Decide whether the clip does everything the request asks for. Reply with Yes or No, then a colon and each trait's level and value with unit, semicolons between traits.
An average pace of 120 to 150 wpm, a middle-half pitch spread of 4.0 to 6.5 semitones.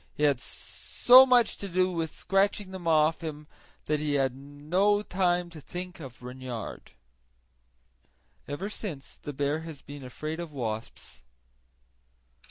Yes: average, 140 wpm; average, 4.5 semitones